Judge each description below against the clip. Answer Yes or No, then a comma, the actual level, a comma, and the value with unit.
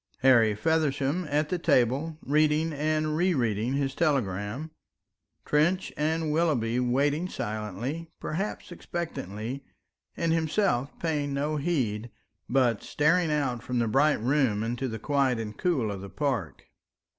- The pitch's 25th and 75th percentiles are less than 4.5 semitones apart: No, average, 4.8 semitones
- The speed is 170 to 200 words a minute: No, slow, 135 wpm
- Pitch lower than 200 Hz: Yes, medium, 140 Hz